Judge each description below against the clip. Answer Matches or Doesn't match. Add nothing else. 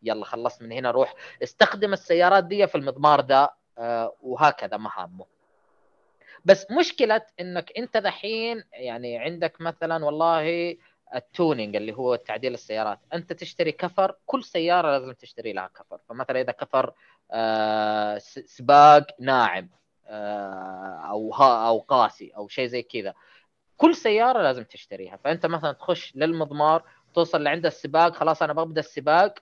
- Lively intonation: Matches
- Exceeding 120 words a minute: Matches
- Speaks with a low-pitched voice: Doesn't match